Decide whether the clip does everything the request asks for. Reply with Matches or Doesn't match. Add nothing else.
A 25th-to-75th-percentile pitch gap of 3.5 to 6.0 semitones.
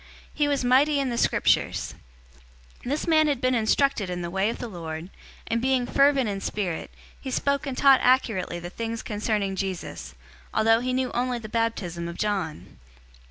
Matches